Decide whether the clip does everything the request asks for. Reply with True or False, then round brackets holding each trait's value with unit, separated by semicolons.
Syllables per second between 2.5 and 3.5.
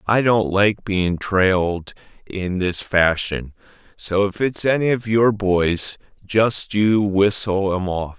True (3.4 syllables/s)